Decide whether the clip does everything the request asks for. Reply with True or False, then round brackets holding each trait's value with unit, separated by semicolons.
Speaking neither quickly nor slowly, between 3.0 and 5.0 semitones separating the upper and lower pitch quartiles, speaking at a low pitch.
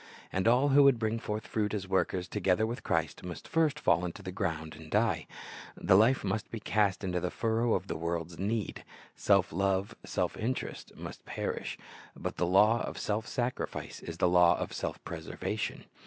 True (185 wpm; 4.2 semitones; 100 Hz)